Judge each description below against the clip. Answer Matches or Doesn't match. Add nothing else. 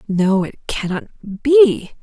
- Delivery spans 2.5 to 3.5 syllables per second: Matches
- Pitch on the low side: Doesn't match